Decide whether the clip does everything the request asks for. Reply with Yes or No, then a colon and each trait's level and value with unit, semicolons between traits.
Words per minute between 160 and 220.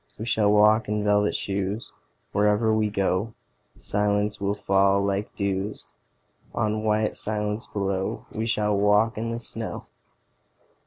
No: slow, 135 wpm